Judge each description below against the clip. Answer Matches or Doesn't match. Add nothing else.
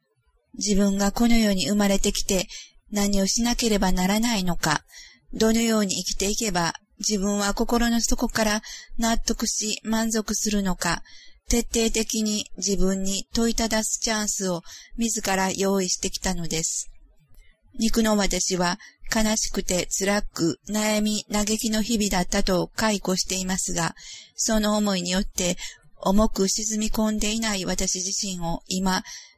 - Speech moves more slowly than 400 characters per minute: Matches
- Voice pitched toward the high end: Matches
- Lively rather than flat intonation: Doesn't match